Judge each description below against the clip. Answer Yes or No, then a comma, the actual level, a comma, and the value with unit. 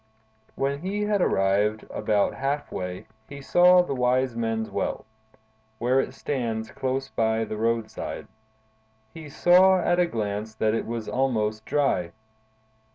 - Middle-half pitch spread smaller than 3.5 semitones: No, average, 4.7 semitones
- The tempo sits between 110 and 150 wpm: Yes, average, 140 wpm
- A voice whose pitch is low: Yes, low, 120 Hz